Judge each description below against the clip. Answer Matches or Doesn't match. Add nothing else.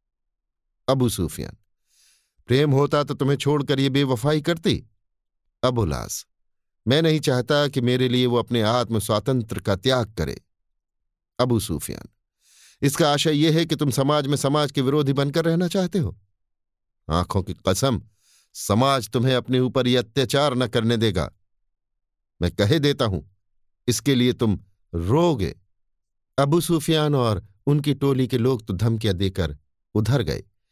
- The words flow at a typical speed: Matches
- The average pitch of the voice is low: Matches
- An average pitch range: Doesn't match